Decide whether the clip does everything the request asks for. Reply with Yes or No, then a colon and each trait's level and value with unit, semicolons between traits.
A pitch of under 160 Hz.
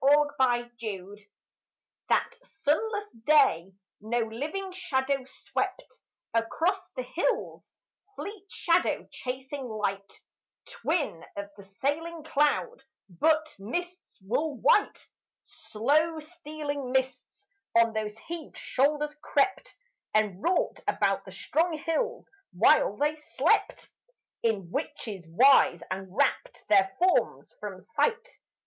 No: very high, 285 Hz